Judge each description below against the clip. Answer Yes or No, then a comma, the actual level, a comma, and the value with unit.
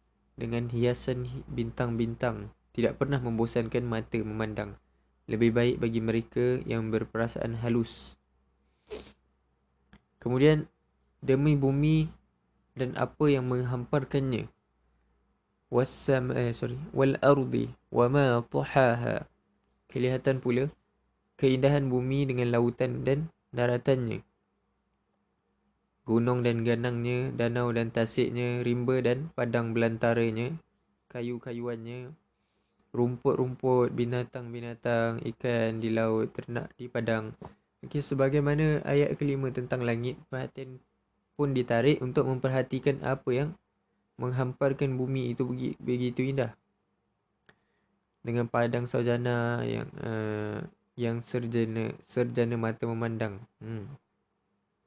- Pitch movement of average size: No, narrow, 2.3 semitones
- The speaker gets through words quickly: No, average, 95 wpm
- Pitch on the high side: No, low, 120 Hz